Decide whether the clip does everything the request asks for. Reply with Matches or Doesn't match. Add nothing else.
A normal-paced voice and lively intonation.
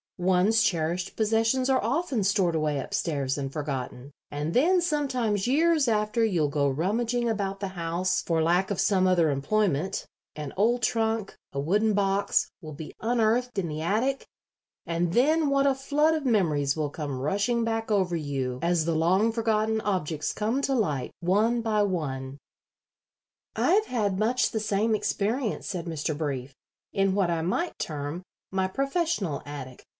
Matches